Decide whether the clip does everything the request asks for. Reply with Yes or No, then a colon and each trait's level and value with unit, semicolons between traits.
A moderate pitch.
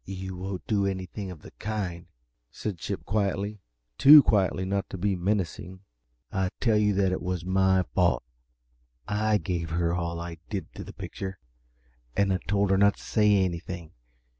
No: very low, 95 Hz